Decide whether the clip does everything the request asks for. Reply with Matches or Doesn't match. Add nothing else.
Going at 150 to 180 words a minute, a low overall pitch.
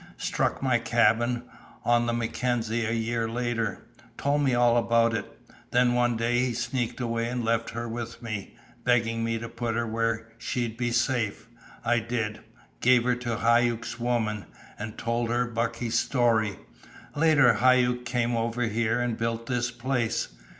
Matches